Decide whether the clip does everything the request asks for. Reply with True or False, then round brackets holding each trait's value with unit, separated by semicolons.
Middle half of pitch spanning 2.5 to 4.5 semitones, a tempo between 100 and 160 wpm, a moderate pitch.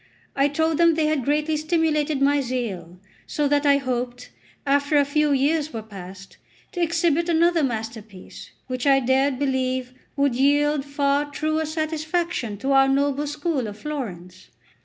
False (3.2 semitones; 155 wpm; 280 Hz)